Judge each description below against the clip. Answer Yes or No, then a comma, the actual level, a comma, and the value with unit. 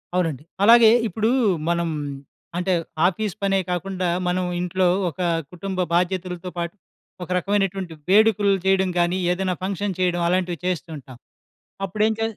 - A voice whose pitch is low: No, medium, 185 Hz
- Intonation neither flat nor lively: No, narrow, 2.0 semitones